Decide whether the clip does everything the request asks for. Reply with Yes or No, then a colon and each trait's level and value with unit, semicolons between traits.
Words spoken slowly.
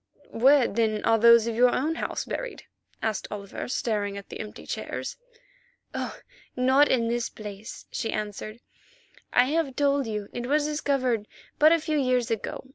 No: average, 165 wpm